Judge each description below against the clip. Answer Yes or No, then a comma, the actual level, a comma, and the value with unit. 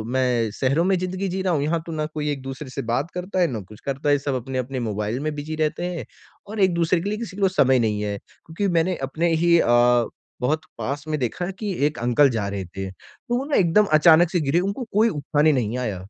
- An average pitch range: No, wide, 5.7 semitones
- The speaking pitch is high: No, medium, 150 Hz